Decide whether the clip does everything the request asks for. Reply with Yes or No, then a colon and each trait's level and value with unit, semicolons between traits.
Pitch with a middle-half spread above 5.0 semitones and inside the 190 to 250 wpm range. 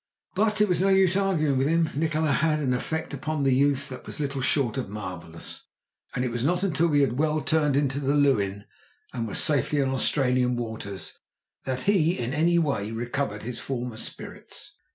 No: average, 4.2 semitones; average, 195 wpm